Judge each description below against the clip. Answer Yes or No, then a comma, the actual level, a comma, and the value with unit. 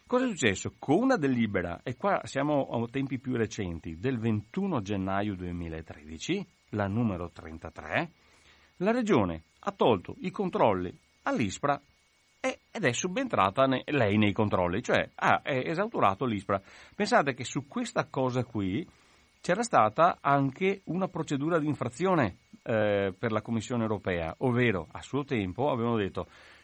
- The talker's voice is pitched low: Yes, low, 115 Hz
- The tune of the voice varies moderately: No, wide, 7.2 semitones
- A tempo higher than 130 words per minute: Yes, average, 140 wpm